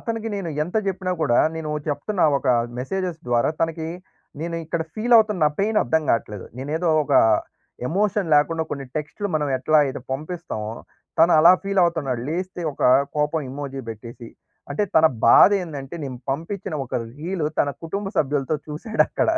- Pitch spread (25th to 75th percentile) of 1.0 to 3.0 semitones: No, average, 4.5 semitones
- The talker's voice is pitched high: No, medium, 160 Hz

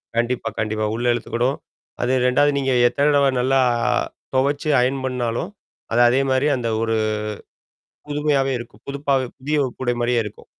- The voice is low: Yes, low, 130 Hz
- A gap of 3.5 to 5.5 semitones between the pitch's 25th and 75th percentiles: No, average, 2.7 semitones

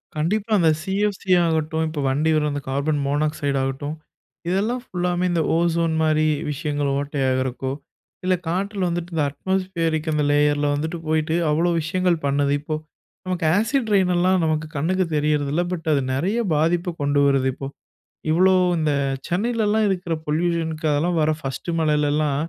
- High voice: No, medium, 160 Hz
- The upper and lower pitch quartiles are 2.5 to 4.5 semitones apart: Yes, average, 3.4 semitones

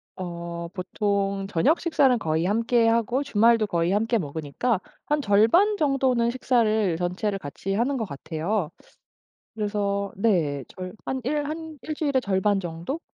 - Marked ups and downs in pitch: Yes, wide, 5.7 semitones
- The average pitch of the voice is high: Yes, high, 210 Hz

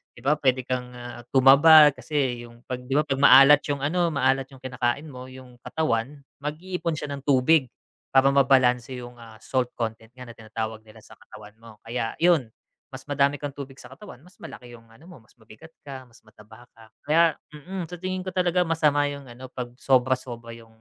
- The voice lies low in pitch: Yes, low, 130 Hz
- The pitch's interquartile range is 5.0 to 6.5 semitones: No, average, 3.6 semitones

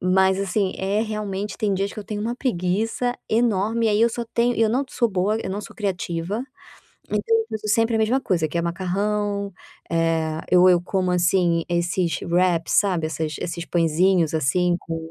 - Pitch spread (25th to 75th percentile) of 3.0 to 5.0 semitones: Yes, average, 3.8 semitones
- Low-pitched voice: No, high, 190 Hz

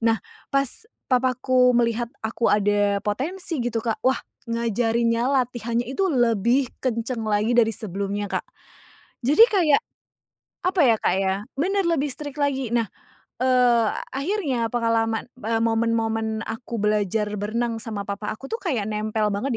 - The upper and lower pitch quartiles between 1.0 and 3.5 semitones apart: Yes, average, 3.0 semitones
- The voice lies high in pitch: Yes, high, 230 Hz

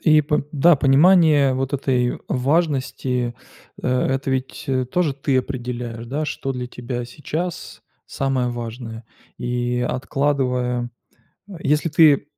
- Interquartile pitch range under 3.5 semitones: Yes, average, 3.0 semitones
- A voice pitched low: Yes, low, 130 Hz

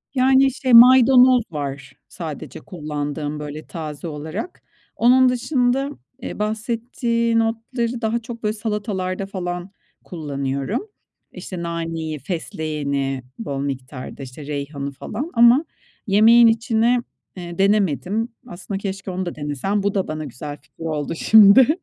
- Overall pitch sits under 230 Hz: Yes, high, 190 Hz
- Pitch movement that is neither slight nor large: No, wide, 7.6 semitones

